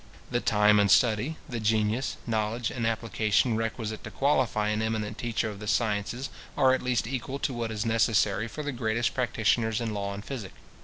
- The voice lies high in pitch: No, low, 110 Hz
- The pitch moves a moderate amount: No, narrow, 2.3 semitones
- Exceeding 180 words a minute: Yes, average, 190 wpm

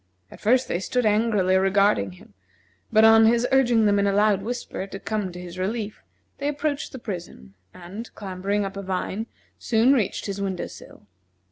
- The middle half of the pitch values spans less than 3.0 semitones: No, average, 3.3 semitones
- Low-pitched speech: No, high, 205 Hz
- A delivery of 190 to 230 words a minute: No, average, 180 wpm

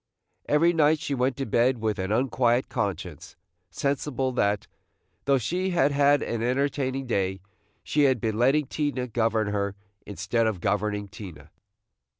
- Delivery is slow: No, average, 150 wpm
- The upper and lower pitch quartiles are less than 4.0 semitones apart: No, average, 4.8 semitones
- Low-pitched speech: Yes, low, 125 Hz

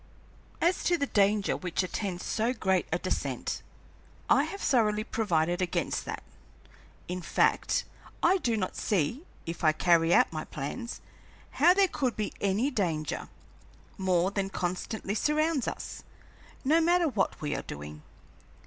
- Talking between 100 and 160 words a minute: Yes, average, 145 wpm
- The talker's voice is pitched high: Yes, high, 200 Hz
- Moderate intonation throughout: No, wide, 6.8 semitones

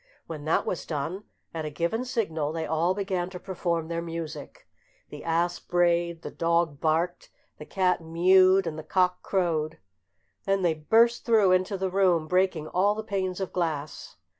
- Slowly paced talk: No, average, 170 wpm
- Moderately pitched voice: Yes, medium, 175 Hz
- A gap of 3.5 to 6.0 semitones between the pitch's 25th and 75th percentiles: No, narrow, 2.6 semitones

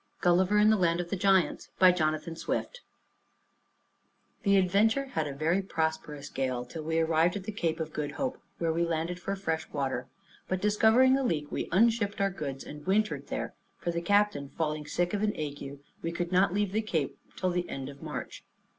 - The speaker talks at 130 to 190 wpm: No, average, 200 wpm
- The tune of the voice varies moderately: Yes, average, 4.3 semitones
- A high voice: No, medium, 175 Hz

